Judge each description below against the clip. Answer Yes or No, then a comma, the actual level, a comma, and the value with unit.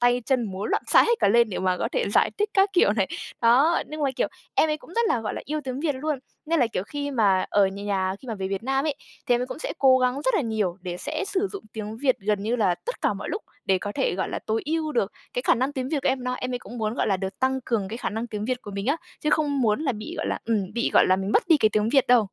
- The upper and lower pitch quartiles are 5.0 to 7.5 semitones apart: Yes, wide, 5.4 semitones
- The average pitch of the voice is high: Yes, high, 245 Hz